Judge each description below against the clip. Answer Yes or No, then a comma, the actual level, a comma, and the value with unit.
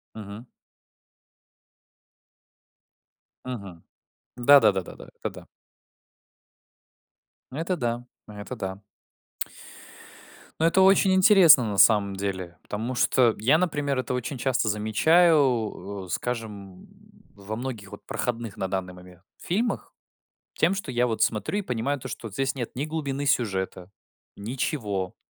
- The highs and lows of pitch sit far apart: Yes, wide, 5.8 semitones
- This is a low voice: Yes, low, 120 Hz